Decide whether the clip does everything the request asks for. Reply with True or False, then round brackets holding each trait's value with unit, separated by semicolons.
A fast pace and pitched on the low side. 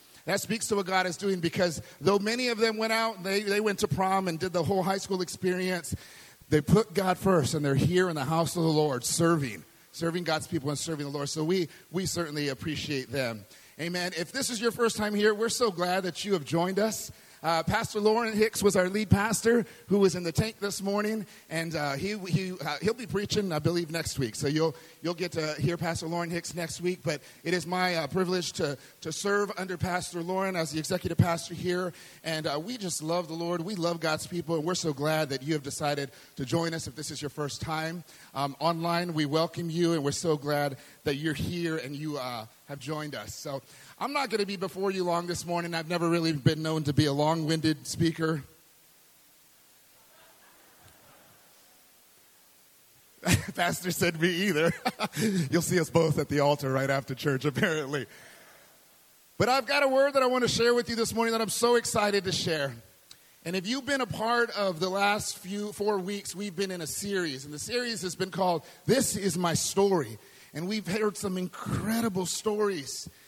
False (215 wpm; 175 Hz)